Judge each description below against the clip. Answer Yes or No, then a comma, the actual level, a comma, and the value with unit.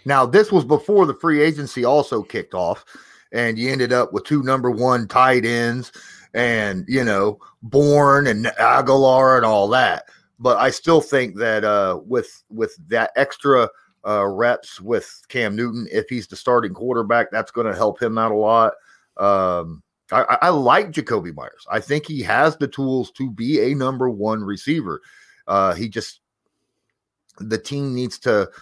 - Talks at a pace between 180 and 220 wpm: No, average, 170 wpm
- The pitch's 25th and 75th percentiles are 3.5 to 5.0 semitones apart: No, average, 3.0 semitones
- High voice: No, low, 125 Hz